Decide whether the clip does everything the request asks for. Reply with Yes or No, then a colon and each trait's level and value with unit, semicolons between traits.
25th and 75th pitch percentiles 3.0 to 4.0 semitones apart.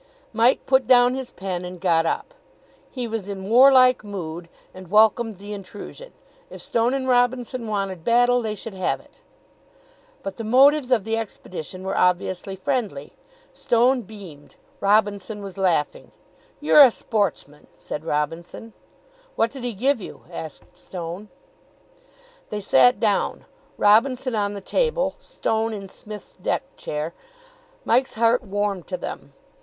No: average, 4.6 semitones